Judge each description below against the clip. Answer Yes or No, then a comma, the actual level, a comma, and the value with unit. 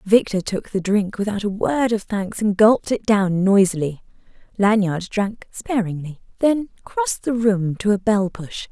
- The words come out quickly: No, average, 170 wpm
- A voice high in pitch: Yes, high, 205 Hz